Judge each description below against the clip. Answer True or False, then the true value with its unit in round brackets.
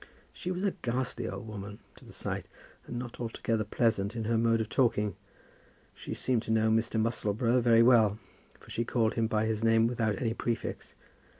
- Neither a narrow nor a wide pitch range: False (1.4 semitones)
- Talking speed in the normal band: True (190 wpm)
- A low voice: True (115 Hz)